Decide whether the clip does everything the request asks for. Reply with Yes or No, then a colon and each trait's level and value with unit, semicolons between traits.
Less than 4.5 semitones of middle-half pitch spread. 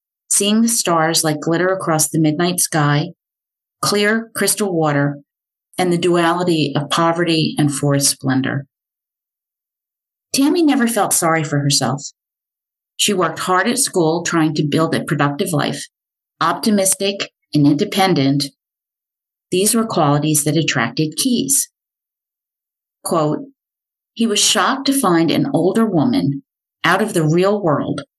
No: average, 5.2 semitones